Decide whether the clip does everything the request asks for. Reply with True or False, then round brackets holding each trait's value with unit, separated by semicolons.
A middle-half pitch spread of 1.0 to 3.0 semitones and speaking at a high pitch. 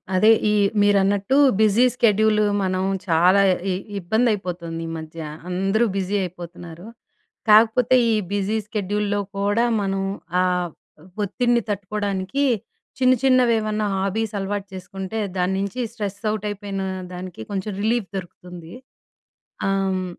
True (2.7 semitones; 200 Hz)